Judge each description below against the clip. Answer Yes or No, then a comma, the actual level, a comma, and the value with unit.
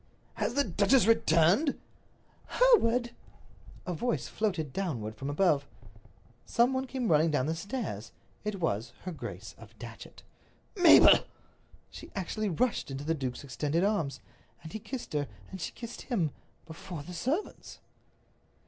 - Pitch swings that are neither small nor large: No, wide, 7.7 semitones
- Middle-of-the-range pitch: Yes, medium, 180 Hz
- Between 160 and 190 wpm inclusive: No, average, 140 wpm